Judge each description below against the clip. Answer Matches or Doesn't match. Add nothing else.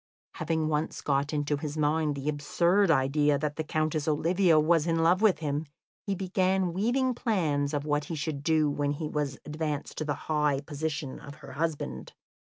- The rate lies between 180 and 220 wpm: Matches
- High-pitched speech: Doesn't match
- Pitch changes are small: Matches